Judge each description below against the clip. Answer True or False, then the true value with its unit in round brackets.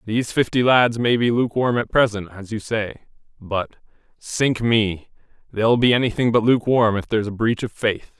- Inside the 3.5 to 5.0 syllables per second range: False (5.2 syllables/s)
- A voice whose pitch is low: True (115 Hz)